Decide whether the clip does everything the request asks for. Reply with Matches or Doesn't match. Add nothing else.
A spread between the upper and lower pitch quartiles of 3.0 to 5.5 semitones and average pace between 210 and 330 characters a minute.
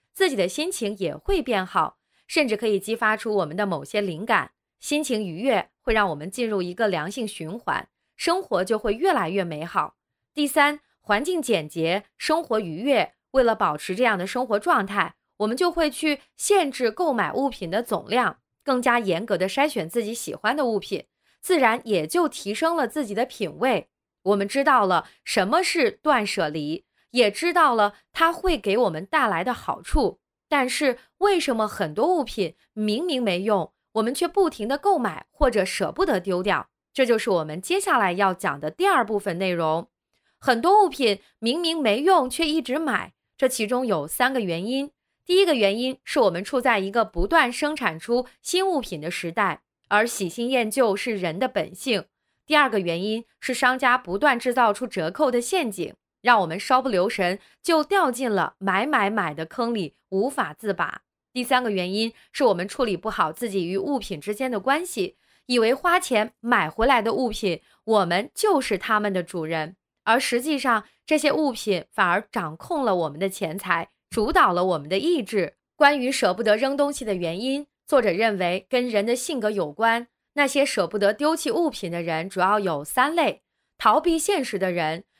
Doesn't match